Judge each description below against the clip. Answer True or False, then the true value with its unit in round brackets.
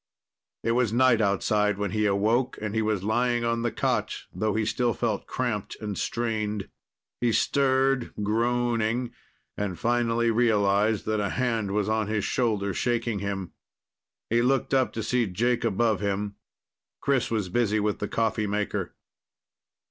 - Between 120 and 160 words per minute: True (155 wpm)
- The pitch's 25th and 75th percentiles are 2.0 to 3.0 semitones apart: True (2.6 semitones)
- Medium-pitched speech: False (110 Hz)